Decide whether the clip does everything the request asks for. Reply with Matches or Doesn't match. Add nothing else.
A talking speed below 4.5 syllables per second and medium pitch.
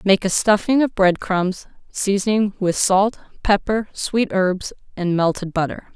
Doesn't match